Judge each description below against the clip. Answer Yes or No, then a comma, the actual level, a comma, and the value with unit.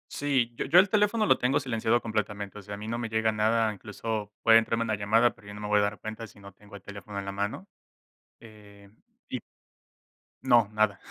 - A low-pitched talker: Yes, low, 110 Hz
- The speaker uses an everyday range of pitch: No, narrow, 2.2 semitones